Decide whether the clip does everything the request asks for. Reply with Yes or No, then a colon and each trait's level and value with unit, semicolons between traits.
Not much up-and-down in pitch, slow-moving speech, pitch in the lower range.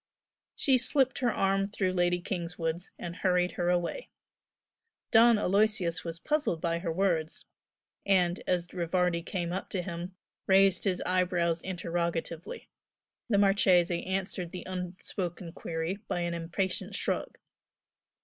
No: narrow, 2.2 semitones; slow, 130 wpm; medium, 180 Hz